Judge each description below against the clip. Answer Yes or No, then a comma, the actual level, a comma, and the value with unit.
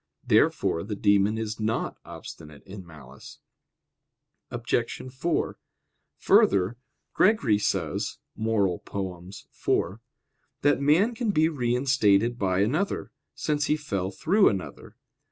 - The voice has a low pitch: Yes, low, 110 Hz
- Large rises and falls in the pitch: Yes, wide, 6.9 semitones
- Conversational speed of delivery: No, slow, 105 wpm